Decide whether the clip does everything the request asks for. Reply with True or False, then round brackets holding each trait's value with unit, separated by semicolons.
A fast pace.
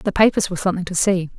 True (260 wpm)